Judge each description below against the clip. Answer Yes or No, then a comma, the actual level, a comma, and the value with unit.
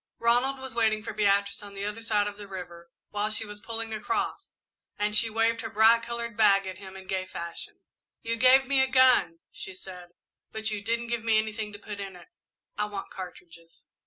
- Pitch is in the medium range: No, high, 210 Hz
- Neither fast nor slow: No, fast, 210 wpm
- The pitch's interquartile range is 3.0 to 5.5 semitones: No, narrow, 2.6 semitones